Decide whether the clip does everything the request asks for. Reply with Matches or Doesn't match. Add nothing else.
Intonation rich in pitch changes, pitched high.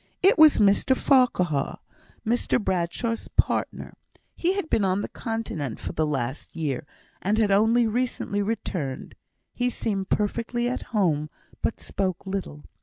Matches